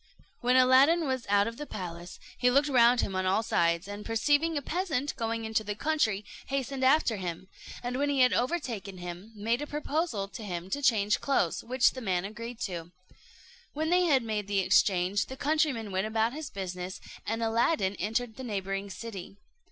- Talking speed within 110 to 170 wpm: No, average, 190 wpm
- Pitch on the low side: No, high, 225 Hz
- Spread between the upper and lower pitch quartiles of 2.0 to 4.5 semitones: No, wide, 5.4 semitones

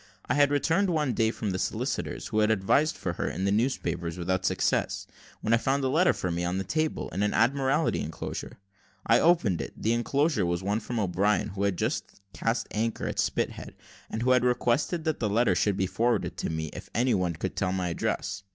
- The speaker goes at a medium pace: No, fast, 215 wpm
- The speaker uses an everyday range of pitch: No, wide, 6.0 semitones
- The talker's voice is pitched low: Yes, low, 110 Hz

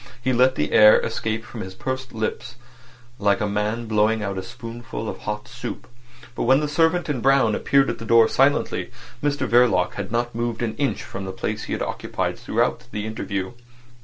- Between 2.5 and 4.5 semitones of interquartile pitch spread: Yes, average, 3.4 semitones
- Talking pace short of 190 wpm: No, average, 200 wpm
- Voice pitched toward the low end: Yes, low, 115 Hz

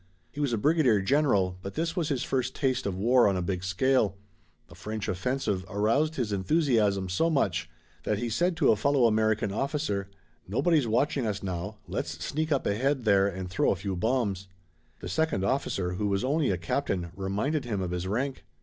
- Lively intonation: Yes, wide, 6.0 semitones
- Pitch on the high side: No, low, 110 Hz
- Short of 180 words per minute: No, average, 195 wpm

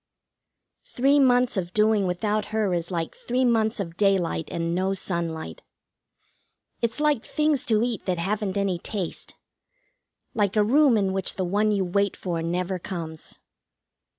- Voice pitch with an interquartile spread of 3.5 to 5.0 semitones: Yes, average, 3.8 semitones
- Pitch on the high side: Yes, high, 200 Hz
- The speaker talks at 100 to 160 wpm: Yes, average, 150 wpm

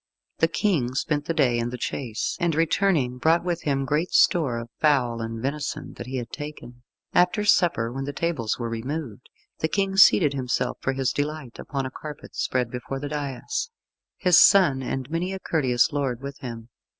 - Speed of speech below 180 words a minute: No, average, 185 wpm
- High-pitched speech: No, medium, 140 Hz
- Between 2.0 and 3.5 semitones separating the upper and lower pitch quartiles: No, average, 4.6 semitones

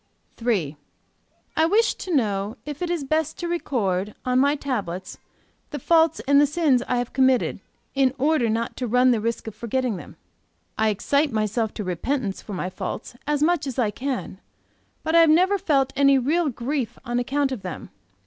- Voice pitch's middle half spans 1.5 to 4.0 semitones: No, average, 5.1 semitones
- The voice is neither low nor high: No, very high, 260 Hz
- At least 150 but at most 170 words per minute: No, average, 190 wpm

